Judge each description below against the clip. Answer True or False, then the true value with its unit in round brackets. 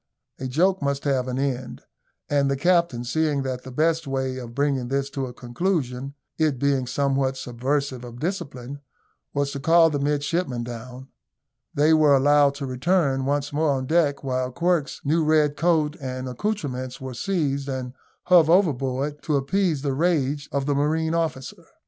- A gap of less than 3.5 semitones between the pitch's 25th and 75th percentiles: True (3.1 semitones)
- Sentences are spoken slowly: False (165 wpm)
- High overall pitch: False (140 Hz)